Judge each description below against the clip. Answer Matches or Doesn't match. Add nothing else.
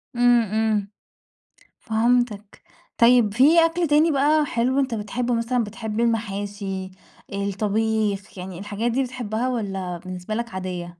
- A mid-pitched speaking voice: Doesn't match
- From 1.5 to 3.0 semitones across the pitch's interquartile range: Doesn't match